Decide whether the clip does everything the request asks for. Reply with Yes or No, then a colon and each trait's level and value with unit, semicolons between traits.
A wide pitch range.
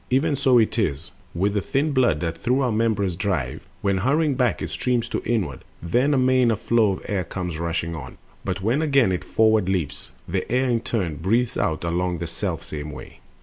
Yes: wide, 6.4 semitones